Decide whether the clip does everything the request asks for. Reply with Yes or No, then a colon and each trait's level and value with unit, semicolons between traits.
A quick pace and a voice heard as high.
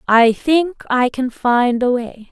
No: average, 180 wpm; very high, 255 Hz